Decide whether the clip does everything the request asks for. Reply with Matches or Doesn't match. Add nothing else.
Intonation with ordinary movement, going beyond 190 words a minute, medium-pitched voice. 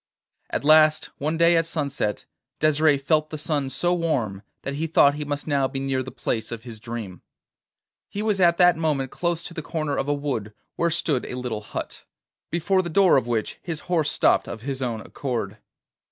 Matches